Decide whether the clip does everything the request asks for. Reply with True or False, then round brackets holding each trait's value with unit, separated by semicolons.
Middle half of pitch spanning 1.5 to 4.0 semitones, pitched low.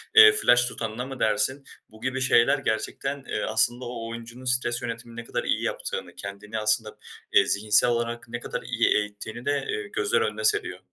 True (3.6 semitones; 120 Hz)